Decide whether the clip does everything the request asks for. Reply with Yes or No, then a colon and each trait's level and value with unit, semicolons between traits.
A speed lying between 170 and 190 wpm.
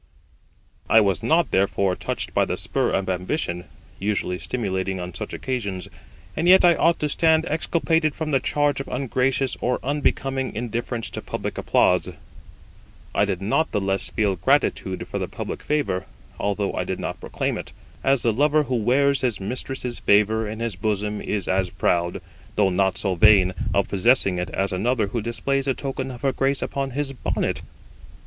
Yes: average, 175 wpm